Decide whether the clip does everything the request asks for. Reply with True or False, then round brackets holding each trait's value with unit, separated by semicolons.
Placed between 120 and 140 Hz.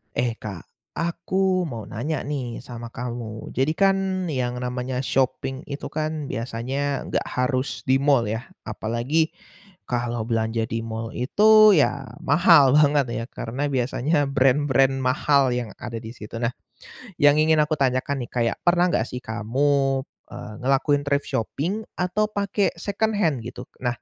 True (135 Hz)